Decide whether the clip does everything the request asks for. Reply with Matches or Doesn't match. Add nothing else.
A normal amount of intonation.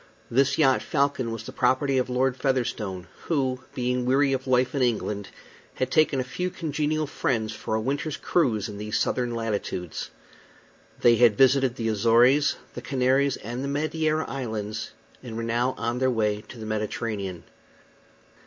Matches